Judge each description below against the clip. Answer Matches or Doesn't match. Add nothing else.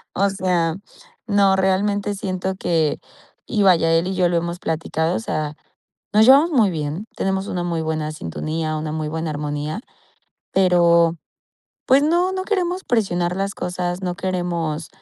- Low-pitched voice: Doesn't match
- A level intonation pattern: Doesn't match